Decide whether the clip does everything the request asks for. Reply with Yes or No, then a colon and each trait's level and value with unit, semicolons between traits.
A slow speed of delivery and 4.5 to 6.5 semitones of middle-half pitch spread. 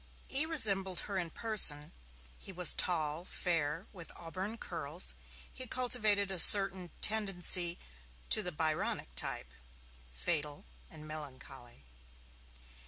Yes: slow, 110 wpm; average, 4.8 semitones